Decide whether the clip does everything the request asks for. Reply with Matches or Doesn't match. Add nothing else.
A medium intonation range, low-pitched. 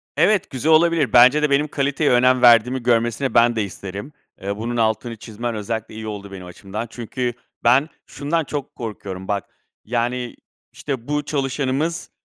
Matches